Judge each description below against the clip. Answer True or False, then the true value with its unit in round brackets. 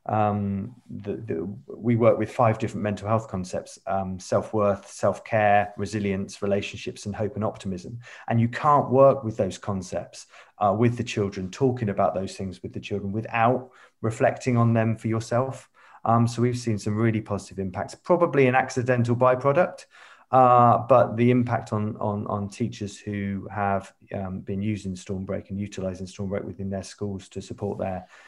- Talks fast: False (170 wpm)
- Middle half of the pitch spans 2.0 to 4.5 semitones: True (3.1 semitones)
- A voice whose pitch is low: True (105 Hz)